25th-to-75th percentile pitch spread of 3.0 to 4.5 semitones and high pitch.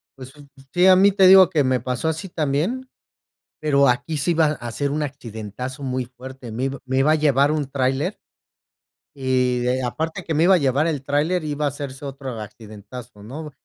No: average, 3.4 semitones; medium, 140 Hz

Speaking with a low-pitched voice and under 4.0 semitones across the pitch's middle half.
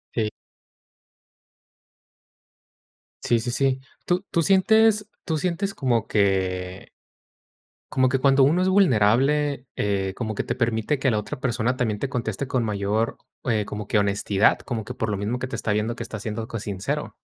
No: low, 115 Hz; average, 4.6 semitones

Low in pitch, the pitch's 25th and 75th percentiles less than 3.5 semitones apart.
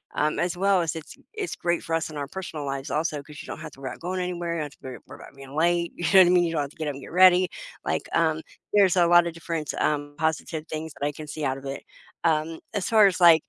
No: medium, 160 Hz; average, 2.7 semitones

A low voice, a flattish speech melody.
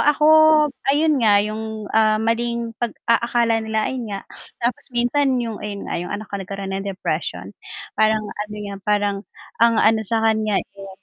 No: high, 220 Hz; narrow, 2.3 semitones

